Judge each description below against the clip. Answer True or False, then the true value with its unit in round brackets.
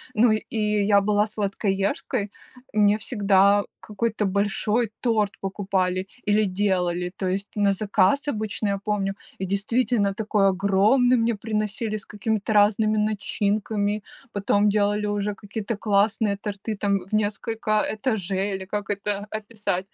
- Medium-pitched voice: False (205 Hz)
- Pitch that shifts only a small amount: True (1.4 semitones)